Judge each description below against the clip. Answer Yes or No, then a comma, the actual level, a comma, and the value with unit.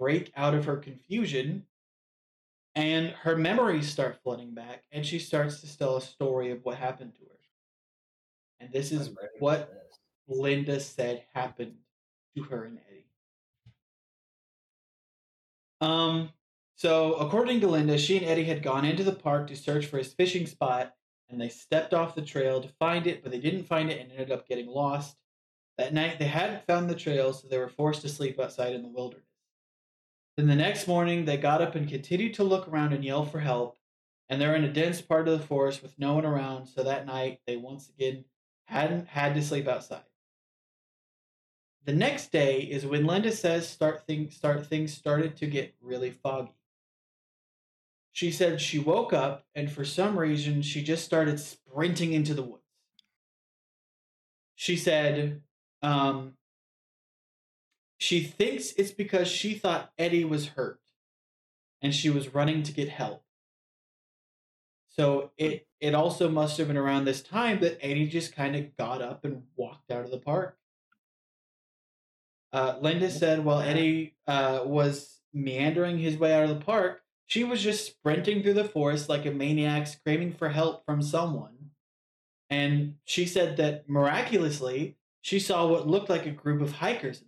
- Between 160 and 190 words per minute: Yes, average, 170 wpm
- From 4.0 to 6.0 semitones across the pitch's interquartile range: No, average, 3.2 semitones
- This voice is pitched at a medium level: Yes, medium, 150 Hz